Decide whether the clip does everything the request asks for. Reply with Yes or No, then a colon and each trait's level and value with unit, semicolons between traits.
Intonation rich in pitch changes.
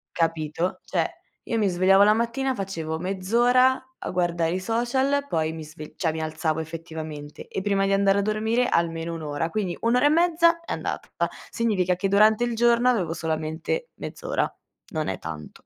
Yes: wide, 6.4 semitones